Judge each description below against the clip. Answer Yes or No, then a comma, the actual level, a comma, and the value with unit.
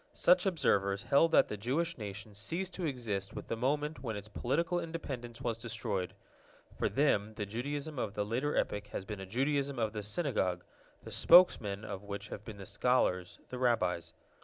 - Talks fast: No, average, 185 wpm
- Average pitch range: No, wide, 5.8 semitones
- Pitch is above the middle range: No, low, 115 Hz